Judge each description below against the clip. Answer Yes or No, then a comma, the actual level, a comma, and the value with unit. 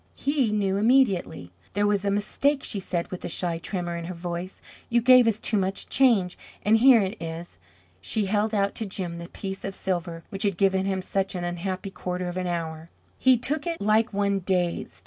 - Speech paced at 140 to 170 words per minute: No, fast, 205 wpm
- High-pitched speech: Yes, high, 195 Hz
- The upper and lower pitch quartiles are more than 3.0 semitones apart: Yes, average, 3.4 semitones